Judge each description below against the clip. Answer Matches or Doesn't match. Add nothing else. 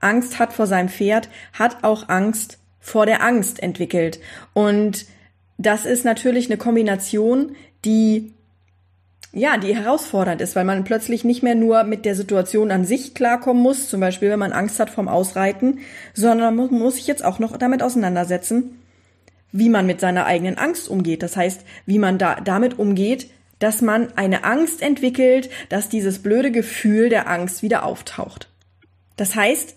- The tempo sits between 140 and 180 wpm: Matches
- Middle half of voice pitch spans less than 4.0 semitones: Doesn't match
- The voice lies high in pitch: Matches